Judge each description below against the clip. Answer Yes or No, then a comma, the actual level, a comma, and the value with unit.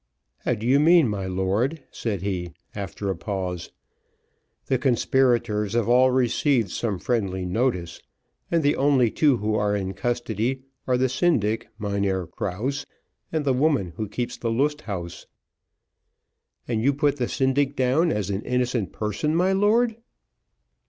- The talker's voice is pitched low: Yes, low, 120 Hz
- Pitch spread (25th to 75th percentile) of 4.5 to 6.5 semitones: Yes, average, 5.3 semitones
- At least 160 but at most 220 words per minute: No, average, 150 wpm